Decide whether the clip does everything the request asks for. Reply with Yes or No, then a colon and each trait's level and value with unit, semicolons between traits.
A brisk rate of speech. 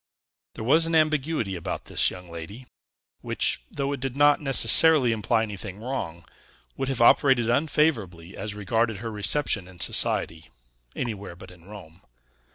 No: average, 150 wpm